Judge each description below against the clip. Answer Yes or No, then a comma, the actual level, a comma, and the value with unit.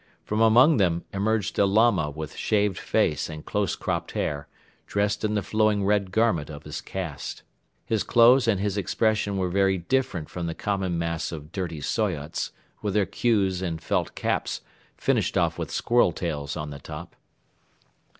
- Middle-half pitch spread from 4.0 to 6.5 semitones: Yes, average, 4.4 semitones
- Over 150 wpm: Yes, average, 170 wpm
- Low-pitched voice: Yes, very low, 95 Hz